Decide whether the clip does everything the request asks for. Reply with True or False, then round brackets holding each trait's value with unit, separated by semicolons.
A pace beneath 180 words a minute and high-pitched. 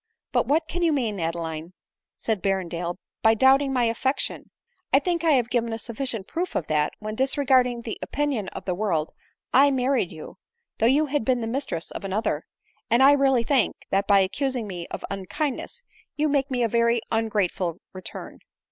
False (185 wpm; 235 Hz)